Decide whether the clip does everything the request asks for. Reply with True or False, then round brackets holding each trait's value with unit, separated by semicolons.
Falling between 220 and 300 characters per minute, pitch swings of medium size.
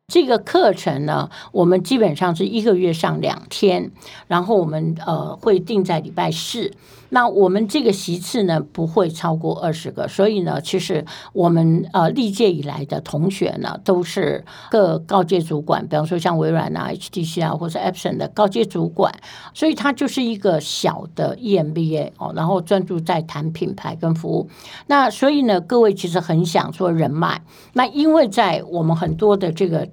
True (275 characters per minute; 4.0 semitones)